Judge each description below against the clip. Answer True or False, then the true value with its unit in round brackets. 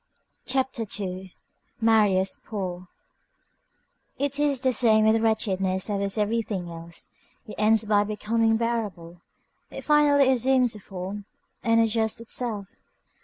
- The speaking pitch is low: False (220 Hz)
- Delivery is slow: True (120 wpm)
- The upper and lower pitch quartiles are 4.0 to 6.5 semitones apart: False (3.2 semitones)